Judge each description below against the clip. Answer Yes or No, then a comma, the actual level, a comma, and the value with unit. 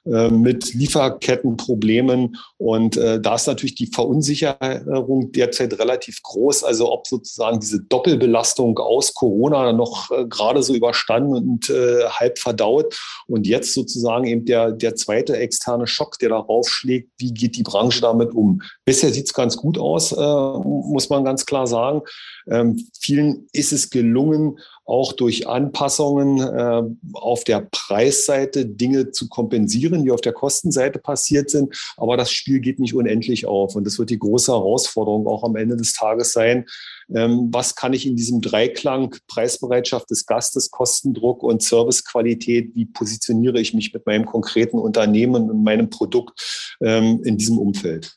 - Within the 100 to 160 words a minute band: Yes, average, 155 wpm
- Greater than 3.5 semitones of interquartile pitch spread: No, average, 2.9 semitones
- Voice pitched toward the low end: Yes, low, 120 Hz